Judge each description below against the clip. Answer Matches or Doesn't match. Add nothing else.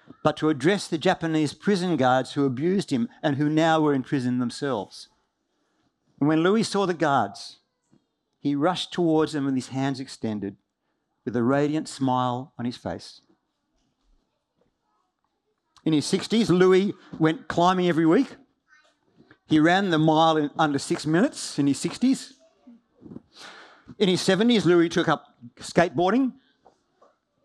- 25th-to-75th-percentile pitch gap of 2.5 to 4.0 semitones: Doesn't match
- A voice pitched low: Doesn't match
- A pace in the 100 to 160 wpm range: Matches